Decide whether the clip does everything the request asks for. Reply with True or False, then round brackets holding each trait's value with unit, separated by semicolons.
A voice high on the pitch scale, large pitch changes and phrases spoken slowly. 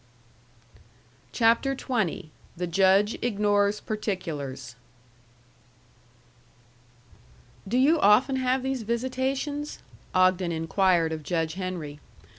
True (205 Hz; 6.8 semitones; 75 wpm)